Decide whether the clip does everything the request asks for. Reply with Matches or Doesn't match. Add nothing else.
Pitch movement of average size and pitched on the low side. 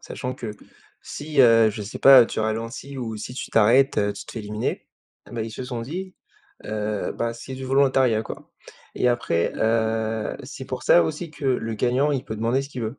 Matches